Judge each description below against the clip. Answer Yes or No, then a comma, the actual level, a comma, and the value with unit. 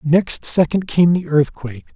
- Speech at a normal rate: Yes, average, 155 wpm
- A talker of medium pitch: Yes, medium, 155 Hz